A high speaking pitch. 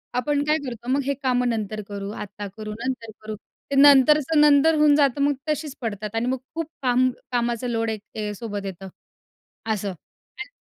Yes: high, 245 Hz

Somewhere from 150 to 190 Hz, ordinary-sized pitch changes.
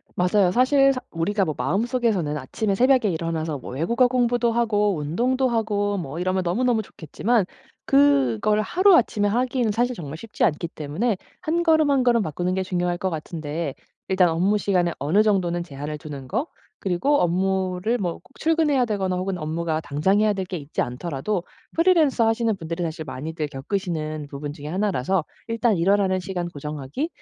No: medium, 185 Hz; wide, 6.3 semitones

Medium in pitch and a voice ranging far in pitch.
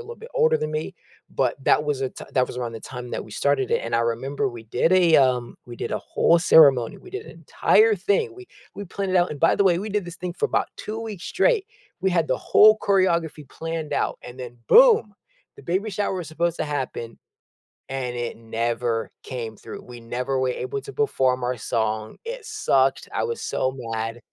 Yes: medium, 150 Hz; wide, 8.6 semitones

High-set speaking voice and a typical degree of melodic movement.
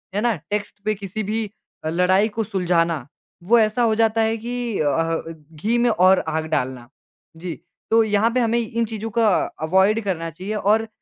Yes: high, 205 Hz; average, 4.6 semitones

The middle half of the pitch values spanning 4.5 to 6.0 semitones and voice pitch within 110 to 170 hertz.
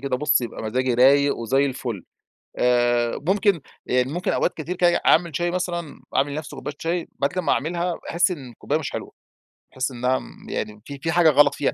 Yes: average, 5.1 semitones; medium, 140 Hz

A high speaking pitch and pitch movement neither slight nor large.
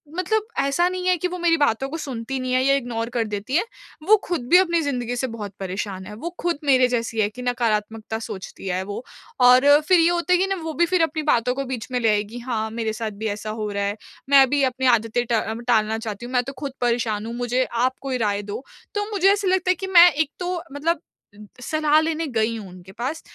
No: very high, 250 Hz; wide, 6.4 semitones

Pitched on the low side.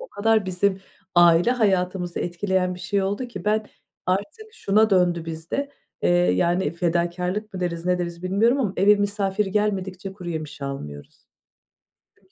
No: medium, 185 Hz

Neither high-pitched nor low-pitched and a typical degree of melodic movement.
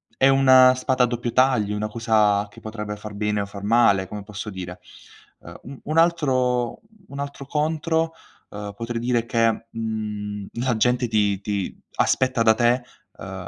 No: low, 115 Hz; average, 3.6 semitones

